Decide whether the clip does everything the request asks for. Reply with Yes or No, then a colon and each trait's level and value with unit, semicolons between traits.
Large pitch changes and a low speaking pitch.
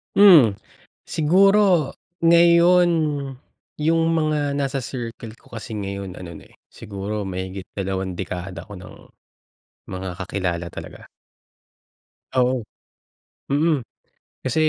Yes: wide, 8.7 semitones; low, 115 Hz